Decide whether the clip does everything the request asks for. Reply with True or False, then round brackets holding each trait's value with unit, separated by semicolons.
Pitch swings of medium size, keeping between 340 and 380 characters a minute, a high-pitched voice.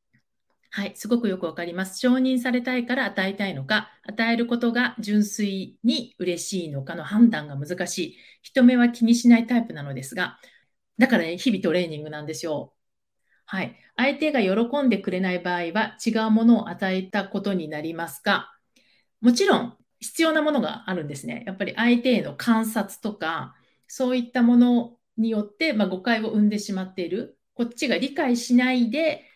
True (4.4 semitones; 355 characters per minute; 220 Hz)